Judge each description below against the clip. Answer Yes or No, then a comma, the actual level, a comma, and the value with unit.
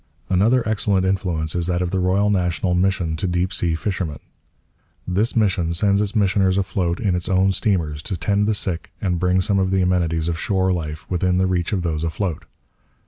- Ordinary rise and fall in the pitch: No, narrow, 2.2 semitones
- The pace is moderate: Yes, average, 195 wpm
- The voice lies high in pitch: No, very low, 90 Hz